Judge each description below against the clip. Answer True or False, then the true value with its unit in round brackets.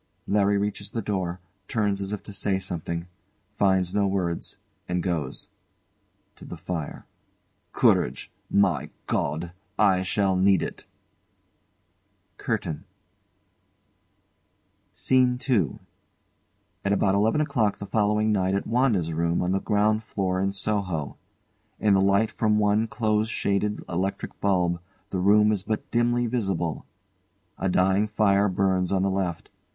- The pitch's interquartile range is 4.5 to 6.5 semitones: False (2.5 semitones)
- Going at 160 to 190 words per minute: False (135 wpm)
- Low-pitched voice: True (100 Hz)